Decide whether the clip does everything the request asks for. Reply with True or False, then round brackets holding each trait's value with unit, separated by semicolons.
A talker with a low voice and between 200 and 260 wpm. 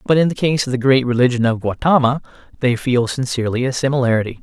True (125 Hz; 205 wpm)